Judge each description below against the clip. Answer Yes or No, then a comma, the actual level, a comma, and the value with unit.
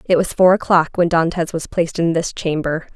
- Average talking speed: No, fast, 225 wpm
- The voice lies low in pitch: No, medium, 170 Hz